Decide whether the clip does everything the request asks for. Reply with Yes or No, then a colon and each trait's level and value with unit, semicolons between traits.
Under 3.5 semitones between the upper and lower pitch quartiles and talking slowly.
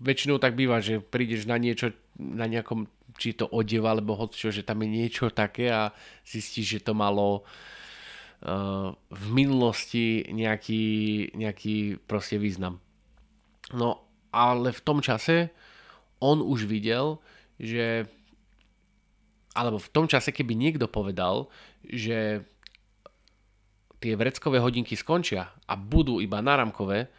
Yes: narrow, 2.6 semitones; slow, 125 wpm